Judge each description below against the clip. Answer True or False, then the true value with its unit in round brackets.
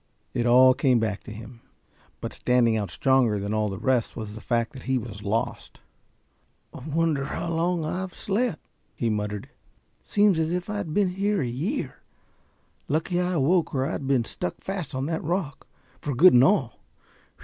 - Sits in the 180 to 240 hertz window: False (135 Hz)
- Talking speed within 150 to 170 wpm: False (180 wpm)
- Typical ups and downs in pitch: False (7.0 semitones)